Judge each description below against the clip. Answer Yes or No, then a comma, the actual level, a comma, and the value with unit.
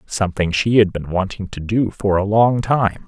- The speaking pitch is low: Yes, low, 100 Hz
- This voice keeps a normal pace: No, fast, 215 wpm